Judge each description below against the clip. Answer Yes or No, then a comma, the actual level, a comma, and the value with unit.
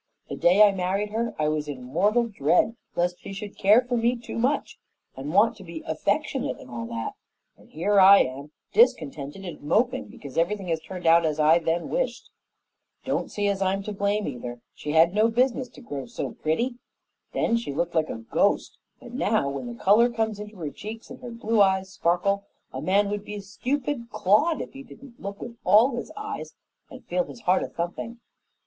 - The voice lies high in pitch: Yes, high, 200 Hz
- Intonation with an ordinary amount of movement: No, wide, 6.0 semitones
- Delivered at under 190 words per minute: No, fast, 205 wpm